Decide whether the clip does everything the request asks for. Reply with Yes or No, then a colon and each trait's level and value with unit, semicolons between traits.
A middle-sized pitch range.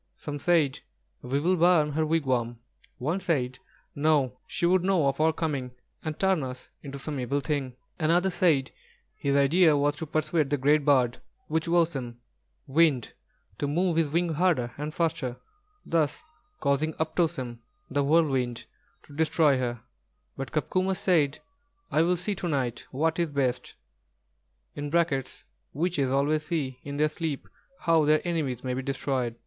Yes: average, 3.6 semitones